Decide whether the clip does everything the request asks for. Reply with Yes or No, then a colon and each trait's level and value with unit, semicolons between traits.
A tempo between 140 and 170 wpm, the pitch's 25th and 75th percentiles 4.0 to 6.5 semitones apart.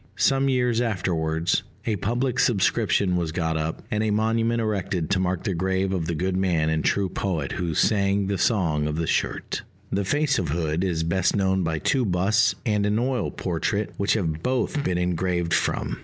No: average, 190 wpm; average, 4.3 semitones